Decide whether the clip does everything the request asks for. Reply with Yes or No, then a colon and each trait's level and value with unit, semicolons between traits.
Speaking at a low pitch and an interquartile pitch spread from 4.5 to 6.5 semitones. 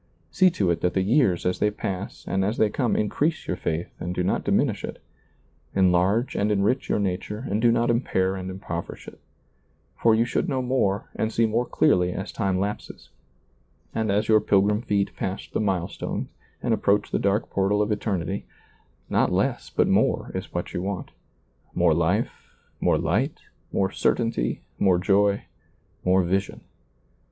No: low, 100 Hz; average, 2.9 semitones